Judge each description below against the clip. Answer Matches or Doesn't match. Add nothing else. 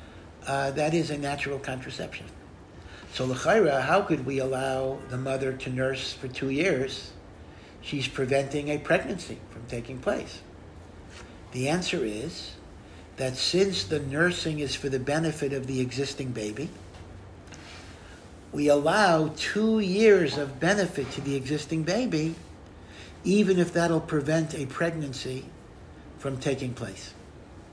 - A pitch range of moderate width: Doesn't match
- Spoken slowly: Matches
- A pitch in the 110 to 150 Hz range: Matches